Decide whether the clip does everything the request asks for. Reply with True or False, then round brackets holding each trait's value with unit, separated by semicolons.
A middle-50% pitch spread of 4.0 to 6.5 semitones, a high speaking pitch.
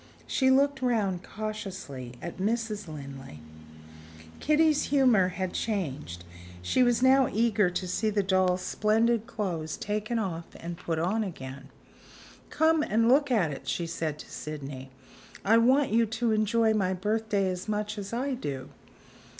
True (5.2 semitones; 210 Hz)